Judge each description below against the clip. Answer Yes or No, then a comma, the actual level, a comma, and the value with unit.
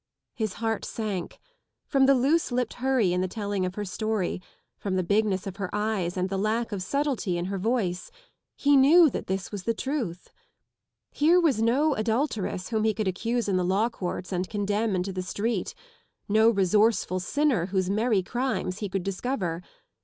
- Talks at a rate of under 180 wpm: No, average, 185 wpm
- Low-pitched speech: No, high, 210 Hz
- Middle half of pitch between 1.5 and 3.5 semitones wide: No, average, 4.2 semitones